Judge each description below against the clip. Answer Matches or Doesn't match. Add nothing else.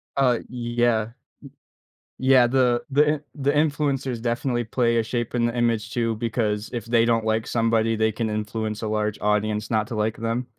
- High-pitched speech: Doesn't match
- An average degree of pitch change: Doesn't match